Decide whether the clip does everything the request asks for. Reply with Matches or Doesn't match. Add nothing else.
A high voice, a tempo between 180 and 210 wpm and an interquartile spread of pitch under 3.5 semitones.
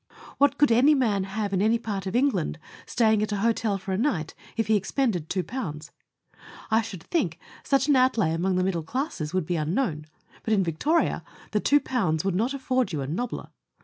Doesn't match